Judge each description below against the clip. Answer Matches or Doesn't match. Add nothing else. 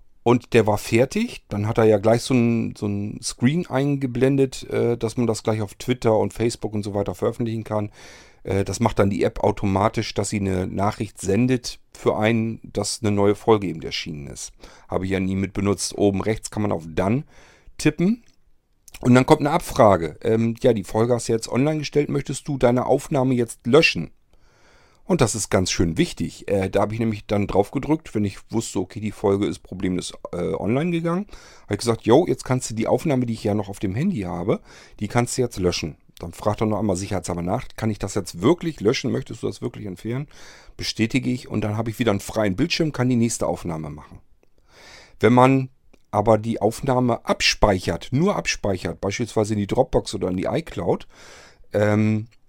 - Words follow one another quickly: Matches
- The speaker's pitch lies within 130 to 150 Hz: Doesn't match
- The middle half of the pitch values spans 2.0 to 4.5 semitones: Matches